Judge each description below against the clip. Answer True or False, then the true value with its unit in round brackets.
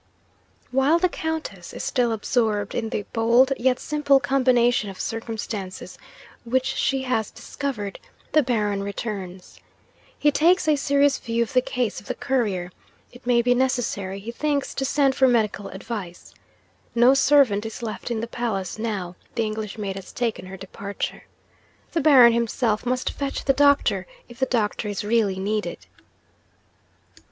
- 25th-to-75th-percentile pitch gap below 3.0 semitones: False (4.2 semitones)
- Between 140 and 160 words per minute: True (155 wpm)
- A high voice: True (235 Hz)